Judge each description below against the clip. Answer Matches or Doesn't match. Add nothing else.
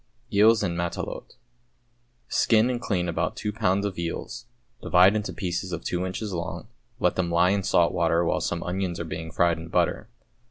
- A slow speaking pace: Doesn't match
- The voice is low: Matches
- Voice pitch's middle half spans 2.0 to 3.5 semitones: Matches